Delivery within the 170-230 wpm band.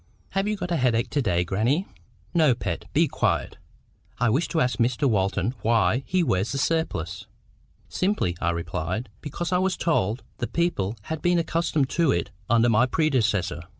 Yes: average, 175 wpm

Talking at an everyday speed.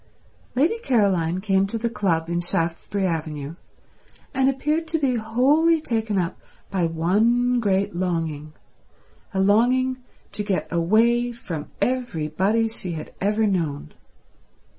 No: slow, 125 wpm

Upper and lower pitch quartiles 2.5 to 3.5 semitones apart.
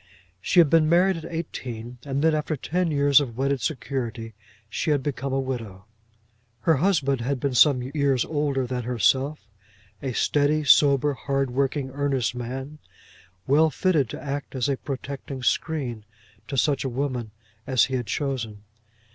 Yes: average, 2.8 semitones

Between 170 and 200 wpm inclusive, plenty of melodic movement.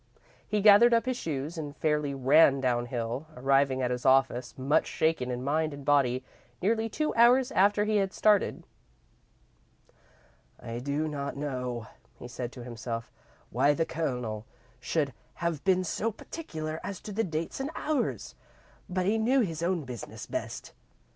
No: average, 155 wpm; wide, 7.3 semitones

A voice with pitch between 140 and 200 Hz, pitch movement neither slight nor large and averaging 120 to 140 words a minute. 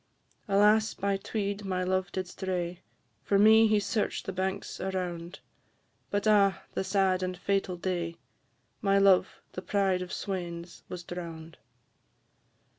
No: high, 190 Hz; narrow, 1.8 semitones; slow, 135 wpm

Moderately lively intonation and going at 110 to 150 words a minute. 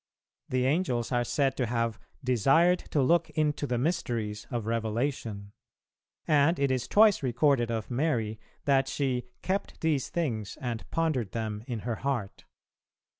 Yes: average, 4.2 semitones; average, 145 wpm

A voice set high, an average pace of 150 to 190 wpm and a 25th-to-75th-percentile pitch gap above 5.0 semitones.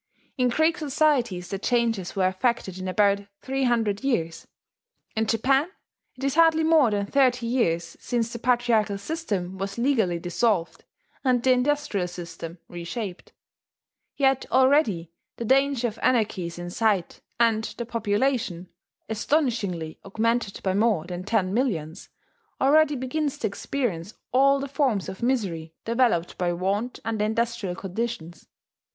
No: high, 225 Hz; average, 140 wpm; wide, 5.6 semitones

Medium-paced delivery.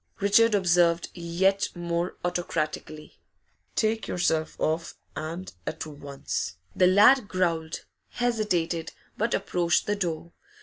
No: slow, 105 wpm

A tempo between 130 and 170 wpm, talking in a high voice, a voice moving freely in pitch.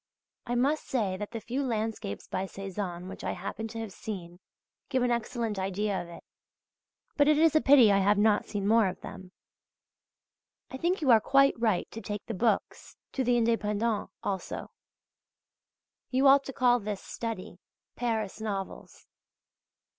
No: average, 165 wpm; high, 220 Hz; average, 3.7 semitones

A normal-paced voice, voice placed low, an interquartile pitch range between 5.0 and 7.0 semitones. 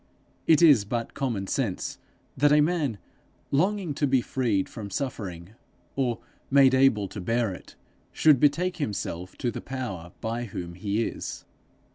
Yes: average, 150 wpm; low, 120 Hz; wide, 5.6 semitones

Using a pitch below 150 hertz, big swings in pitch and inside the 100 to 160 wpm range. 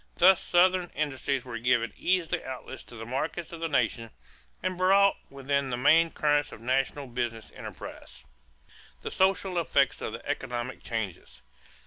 Yes: medium, 140 Hz; wide, 5.8 semitones; average, 150 wpm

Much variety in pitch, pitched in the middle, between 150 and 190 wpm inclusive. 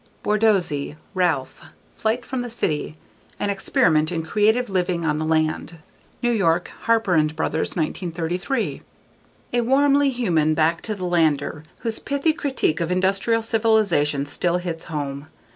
No: wide, 6.0 semitones; medium, 180 Hz; average, 140 wpm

